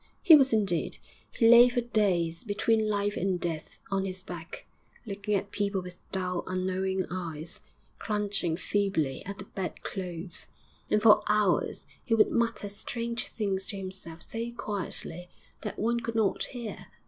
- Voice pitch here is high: Yes, high, 200 Hz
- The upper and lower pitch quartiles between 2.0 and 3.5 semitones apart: Yes, average, 3.0 semitones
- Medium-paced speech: Yes, average, 155 wpm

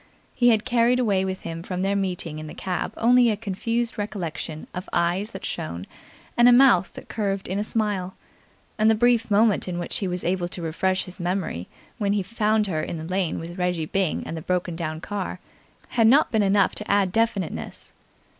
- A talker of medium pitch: No, high, 195 Hz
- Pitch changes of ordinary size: Yes, average, 3.7 semitones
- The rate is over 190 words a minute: Yes, fast, 205 wpm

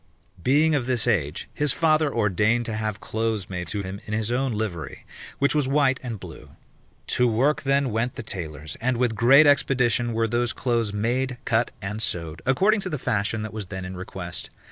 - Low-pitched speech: Yes, low, 115 Hz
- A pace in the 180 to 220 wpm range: Yes, average, 195 wpm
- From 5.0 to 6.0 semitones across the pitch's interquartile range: No, average, 4.2 semitones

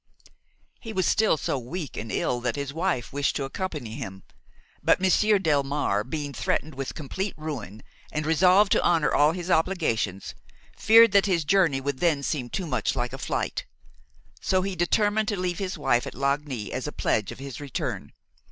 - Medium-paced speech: Yes, average, 180 wpm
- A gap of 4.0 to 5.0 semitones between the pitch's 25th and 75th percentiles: No, wide, 5.6 semitones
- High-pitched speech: No, medium, 150 Hz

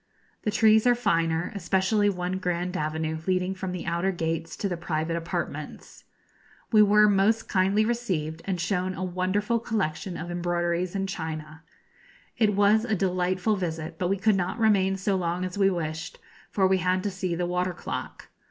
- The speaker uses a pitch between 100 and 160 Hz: No, medium, 185 Hz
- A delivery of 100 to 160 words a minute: No, average, 175 wpm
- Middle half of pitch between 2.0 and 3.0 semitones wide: Yes, average, 2.7 semitones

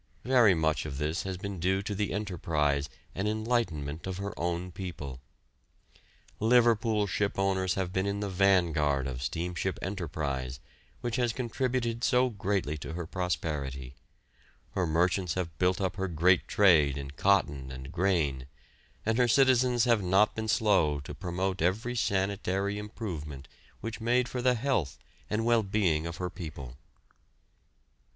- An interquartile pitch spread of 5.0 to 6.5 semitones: Yes, wide, 5.4 semitones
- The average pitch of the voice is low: Yes, very low, 95 Hz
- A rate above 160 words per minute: No, average, 145 wpm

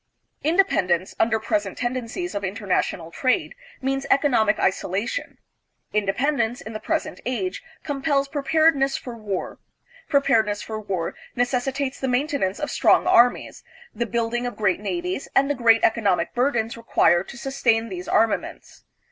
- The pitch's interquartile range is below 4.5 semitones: No, average, 4.8 semitones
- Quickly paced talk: No, average, 140 wpm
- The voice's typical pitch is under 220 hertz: No, high, 235 Hz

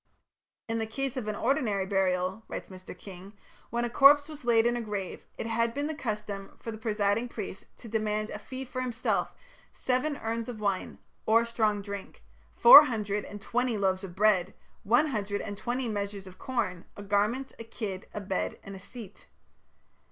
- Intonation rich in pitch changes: No, average, 3.2 semitones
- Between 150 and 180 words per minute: No, average, 190 wpm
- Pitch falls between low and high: No, high, 215 Hz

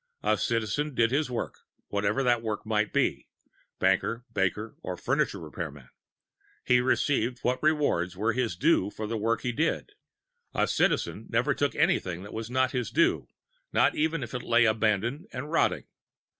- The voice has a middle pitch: No, low, 115 Hz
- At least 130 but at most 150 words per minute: No, average, 165 wpm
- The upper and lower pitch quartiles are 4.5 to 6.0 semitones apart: No, average, 3.6 semitones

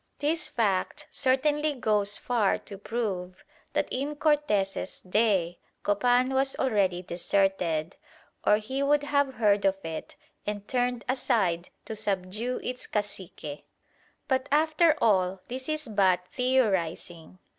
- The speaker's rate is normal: No, slow, 125 wpm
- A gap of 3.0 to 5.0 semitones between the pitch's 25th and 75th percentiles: No, wide, 5.6 semitones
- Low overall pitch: No, high, 215 Hz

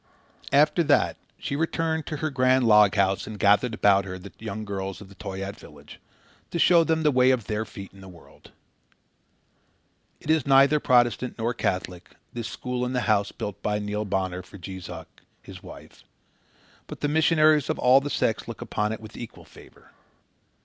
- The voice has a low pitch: Yes, low, 110 Hz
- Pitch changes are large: Yes, wide, 5.8 semitones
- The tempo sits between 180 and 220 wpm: Yes, average, 185 wpm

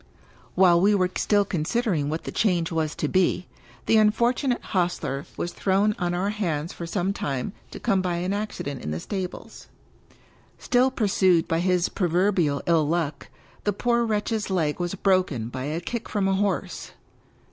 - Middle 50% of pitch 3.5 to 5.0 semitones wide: Yes, average, 3.8 semitones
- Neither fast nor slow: Yes, average, 170 wpm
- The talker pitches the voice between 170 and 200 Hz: Yes, medium, 185 Hz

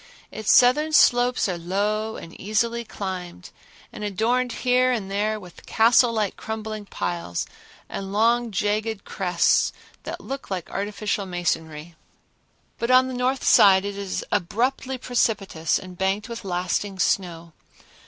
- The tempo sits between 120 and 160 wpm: Yes, slow, 135 wpm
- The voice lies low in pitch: No, high, 210 Hz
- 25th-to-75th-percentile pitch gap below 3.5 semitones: No, average, 4.2 semitones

